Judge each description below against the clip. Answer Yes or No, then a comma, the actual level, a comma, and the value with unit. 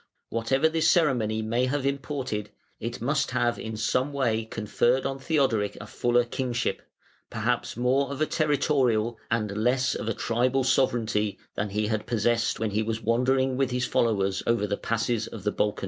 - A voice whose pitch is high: No, low, 120 Hz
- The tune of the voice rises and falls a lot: No, average, 3.2 semitones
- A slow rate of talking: No, average, 175 wpm